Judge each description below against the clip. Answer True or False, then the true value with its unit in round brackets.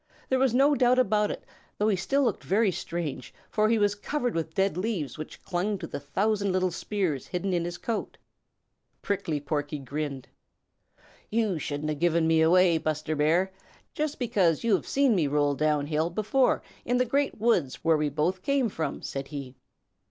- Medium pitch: True (180 Hz)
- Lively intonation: True (6.0 semitones)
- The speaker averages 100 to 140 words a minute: False (185 wpm)